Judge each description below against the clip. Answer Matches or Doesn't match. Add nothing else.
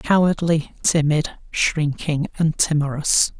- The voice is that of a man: Matches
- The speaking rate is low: Matches